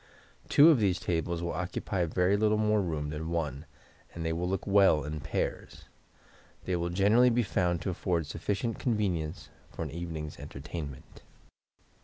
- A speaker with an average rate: Yes, average, 155 wpm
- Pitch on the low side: Yes, very low, 85 Hz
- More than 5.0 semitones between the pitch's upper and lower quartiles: No, average, 3.8 semitones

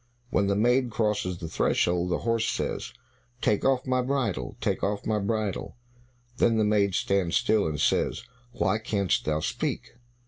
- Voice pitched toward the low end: Yes, low, 105 Hz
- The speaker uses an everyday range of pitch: Yes, average, 3.9 semitones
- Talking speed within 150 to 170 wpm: Yes, average, 165 wpm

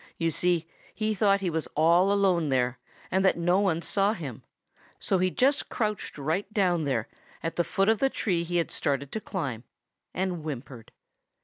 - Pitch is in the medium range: Yes, medium, 175 Hz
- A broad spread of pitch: No, average, 4.2 semitones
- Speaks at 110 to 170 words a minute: No, average, 185 wpm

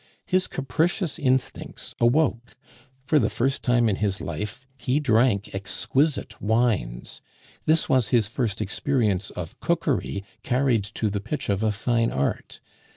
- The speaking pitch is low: Yes, low, 120 Hz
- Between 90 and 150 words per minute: Yes, average, 140 wpm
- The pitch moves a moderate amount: Yes, average, 5.0 semitones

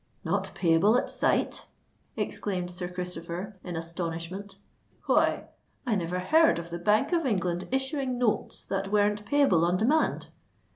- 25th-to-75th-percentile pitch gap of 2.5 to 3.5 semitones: No, average, 4.2 semitones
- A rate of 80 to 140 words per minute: Yes, slow, 135 wpm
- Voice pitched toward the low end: No, high, 190 Hz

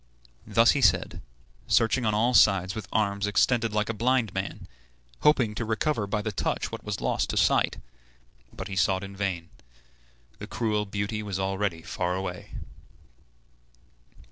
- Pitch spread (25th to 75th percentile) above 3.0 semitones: No, average, 2.7 semitones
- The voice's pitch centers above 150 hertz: No, low, 105 Hz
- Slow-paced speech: No, average, 155 wpm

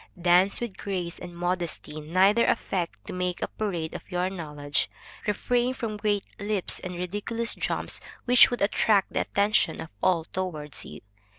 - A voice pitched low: No, medium, 185 Hz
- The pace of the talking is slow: No, average, 160 wpm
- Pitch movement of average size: Yes, average, 3.2 semitones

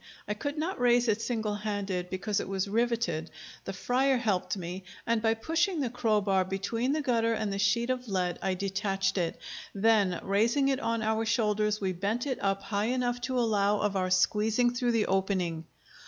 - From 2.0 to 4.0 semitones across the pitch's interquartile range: Yes, average, 3.7 semitones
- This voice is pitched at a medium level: No, high, 215 Hz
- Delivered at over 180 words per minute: Yes, average, 190 wpm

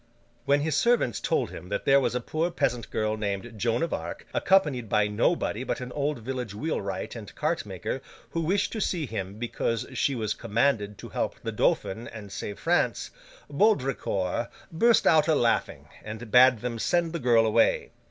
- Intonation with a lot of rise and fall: Yes, wide, 5.8 semitones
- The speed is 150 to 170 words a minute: No, average, 180 wpm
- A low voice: Yes, low, 120 Hz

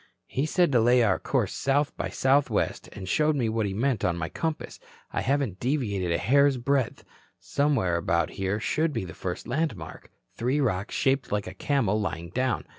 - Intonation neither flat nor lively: No, wide, 6.7 semitones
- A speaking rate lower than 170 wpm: No, average, 190 wpm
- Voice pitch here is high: No, low, 120 Hz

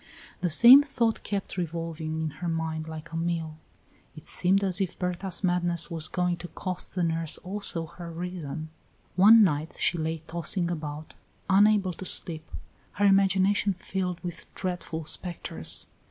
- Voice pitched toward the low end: No, medium, 175 Hz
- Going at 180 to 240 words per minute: No, average, 155 wpm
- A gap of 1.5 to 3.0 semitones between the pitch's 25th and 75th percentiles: Yes, average, 2.7 semitones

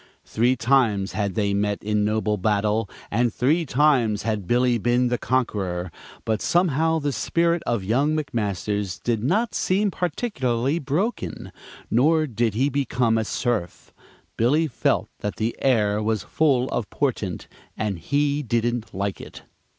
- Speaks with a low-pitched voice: Yes, low, 120 Hz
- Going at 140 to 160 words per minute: Yes, average, 145 wpm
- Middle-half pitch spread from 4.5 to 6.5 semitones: Yes, average, 5.2 semitones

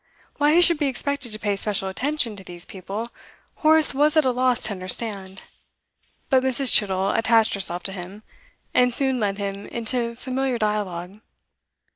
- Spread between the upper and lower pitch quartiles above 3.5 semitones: Yes, average, 5.0 semitones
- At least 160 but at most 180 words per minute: Yes, average, 165 wpm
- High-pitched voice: Yes, high, 225 Hz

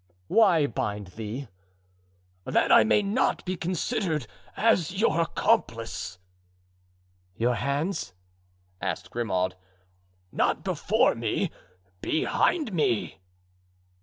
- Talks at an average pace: No, slow, 90 wpm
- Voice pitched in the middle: Yes, medium, 145 Hz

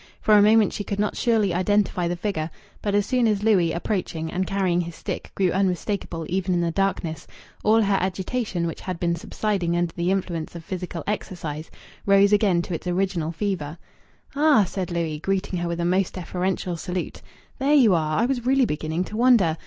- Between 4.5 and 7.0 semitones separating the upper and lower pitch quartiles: No, average, 3.2 semitones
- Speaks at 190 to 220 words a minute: Yes, average, 195 wpm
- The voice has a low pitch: No, medium, 185 Hz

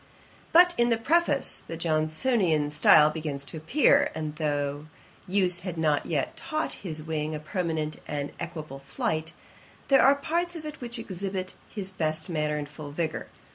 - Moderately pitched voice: Yes, medium, 160 Hz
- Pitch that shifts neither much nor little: No, wide, 6.9 semitones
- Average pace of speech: Yes, average, 165 wpm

